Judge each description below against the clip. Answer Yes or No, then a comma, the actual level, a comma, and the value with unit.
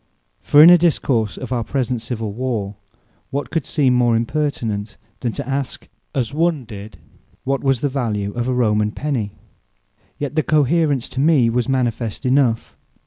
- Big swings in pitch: No, average, 3.9 semitones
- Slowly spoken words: No, average, 165 wpm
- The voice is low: Yes, low, 125 Hz